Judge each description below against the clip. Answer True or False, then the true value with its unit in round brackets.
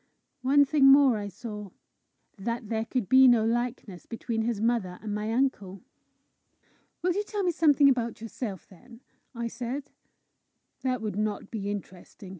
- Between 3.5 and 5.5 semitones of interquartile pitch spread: True (3.9 semitones)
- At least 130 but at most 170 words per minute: True (155 wpm)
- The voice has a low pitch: False (230 Hz)